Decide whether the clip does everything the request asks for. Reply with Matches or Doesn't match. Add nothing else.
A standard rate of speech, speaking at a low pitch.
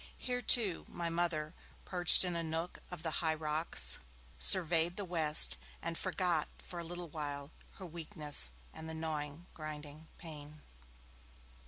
Doesn't match